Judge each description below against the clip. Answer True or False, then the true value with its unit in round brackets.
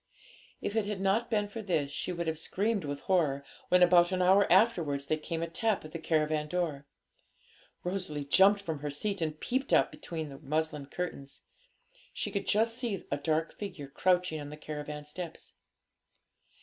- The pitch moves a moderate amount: True (4.5 semitones)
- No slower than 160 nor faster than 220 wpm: True (180 wpm)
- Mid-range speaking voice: True (170 Hz)